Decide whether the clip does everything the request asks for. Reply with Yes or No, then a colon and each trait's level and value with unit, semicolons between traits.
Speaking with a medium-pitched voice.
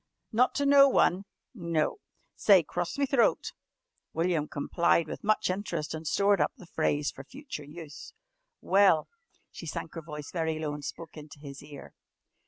Yes: medium, 165 Hz